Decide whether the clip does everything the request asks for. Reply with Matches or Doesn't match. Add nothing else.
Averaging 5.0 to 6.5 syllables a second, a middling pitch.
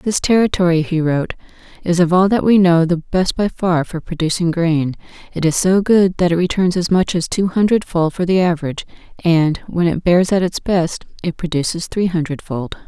Matches